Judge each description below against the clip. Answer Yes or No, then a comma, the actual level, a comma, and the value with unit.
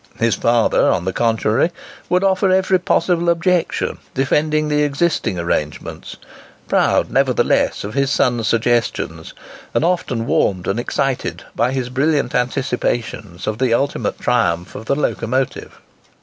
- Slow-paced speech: Yes, slow, 130 wpm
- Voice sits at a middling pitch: No, low, 125 Hz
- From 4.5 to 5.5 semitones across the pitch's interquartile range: Yes, average, 5.1 semitones